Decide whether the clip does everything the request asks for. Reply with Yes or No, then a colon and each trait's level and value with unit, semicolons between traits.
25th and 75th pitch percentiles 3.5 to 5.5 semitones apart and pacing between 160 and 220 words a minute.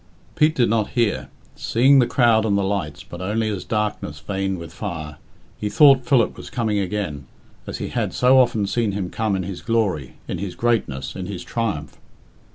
Yes: average, 4.2 semitones; average, 190 wpm